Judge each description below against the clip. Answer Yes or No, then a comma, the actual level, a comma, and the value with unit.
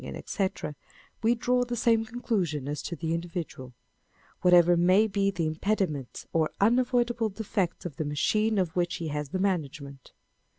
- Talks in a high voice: No, medium, 180 Hz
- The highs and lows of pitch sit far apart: Yes, wide, 5.7 semitones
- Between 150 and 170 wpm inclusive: Yes, average, 160 wpm